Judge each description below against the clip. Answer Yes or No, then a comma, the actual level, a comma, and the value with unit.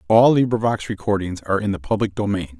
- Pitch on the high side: No, low, 100 Hz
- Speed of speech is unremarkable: Yes, average, 185 wpm